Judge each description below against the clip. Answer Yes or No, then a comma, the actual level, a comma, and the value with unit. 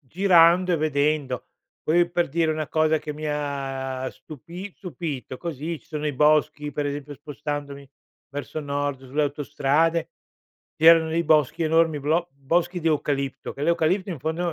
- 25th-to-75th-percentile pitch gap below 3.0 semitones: Yes, narrow, 2.6 semitones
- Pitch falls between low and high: Yes, medium, 150 Hz